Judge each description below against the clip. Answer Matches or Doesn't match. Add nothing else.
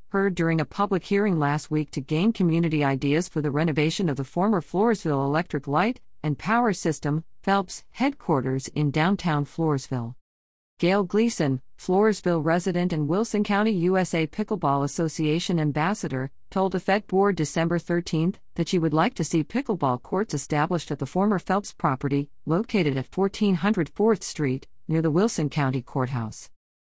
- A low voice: Doesn't match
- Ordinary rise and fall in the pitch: Matches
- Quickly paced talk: Doesn't match